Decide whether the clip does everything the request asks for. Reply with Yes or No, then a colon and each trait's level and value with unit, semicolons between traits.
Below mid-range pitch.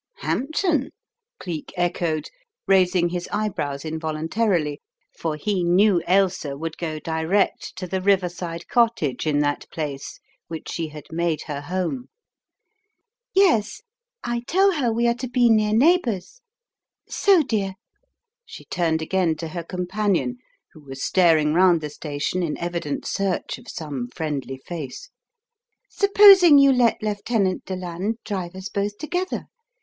No: medium, 185 Hz